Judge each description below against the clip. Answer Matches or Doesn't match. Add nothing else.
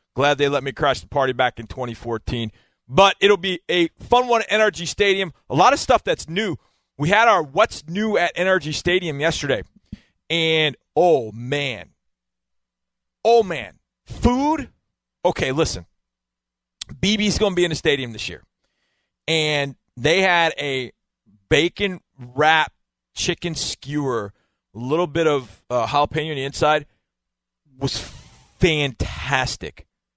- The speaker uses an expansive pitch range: Matches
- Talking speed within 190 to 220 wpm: Doesn't match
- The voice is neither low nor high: Matches